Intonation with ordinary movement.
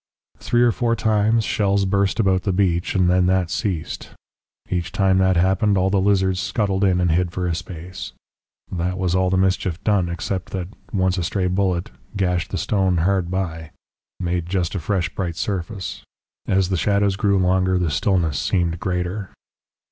No: narrow, 1.8 semitones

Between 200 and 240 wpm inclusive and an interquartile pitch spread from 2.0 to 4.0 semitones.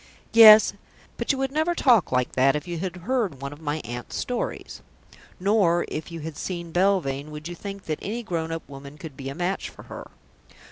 No: fast, 205 wpm; wide, 5.4 semitones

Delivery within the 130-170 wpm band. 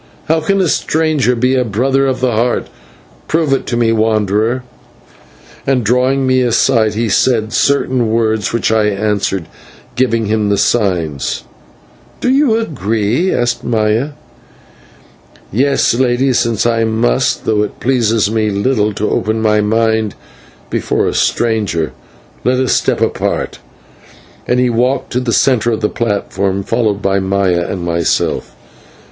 Yes: average, 145 wpm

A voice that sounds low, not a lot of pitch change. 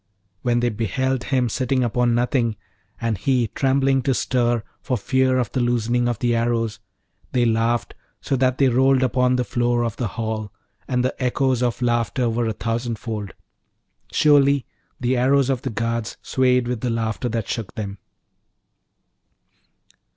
Yes: low, 120 Hz; narrow, 2.0 semitones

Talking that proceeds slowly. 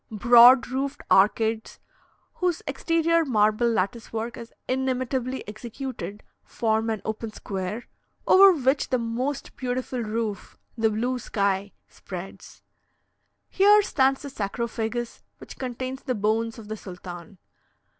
Yes: slow, 120 wpm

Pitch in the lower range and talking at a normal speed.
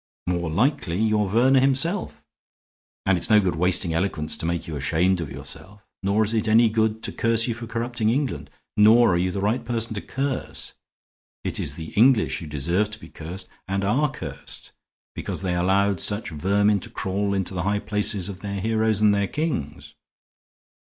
Yes: low, 100 Hz; average, 190 wpm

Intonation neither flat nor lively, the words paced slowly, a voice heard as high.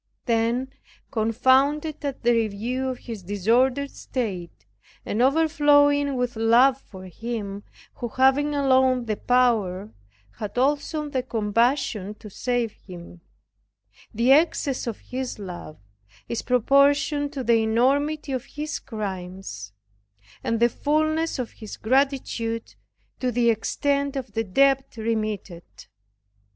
Yes: average, 4.0 semitones; slow, 120 wpm; high, 245 Hz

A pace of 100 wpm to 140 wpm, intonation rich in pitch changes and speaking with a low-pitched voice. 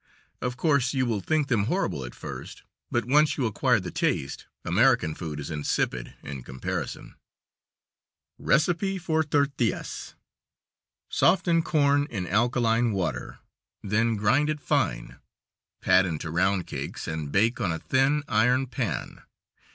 Yes: slow, 135 wpm; wide, 7.7 semitones; low, 120 Hz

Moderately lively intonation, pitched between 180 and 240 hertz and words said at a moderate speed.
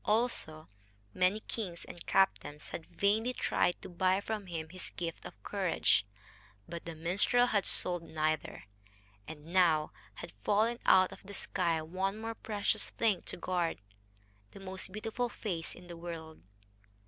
Yes: average, 3.7 semitones; medium, 185 Hz; average, 150 wpm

